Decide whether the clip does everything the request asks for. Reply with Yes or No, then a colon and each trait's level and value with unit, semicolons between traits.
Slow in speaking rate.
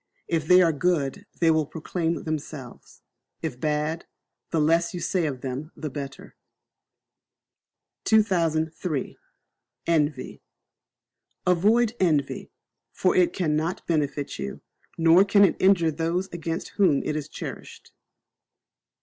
Yes: slow, 115 wpm